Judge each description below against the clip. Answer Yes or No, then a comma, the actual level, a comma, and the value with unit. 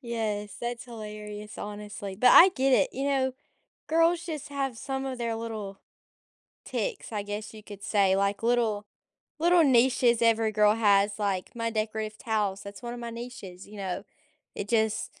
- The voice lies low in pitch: No, high, 220 Hz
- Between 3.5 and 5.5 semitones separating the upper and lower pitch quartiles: No, average, 3.1 semitones